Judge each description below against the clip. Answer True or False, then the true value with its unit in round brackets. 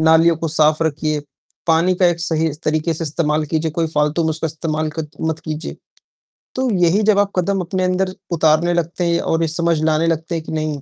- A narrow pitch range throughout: True (1.6 semitones)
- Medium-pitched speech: True (160 Hz)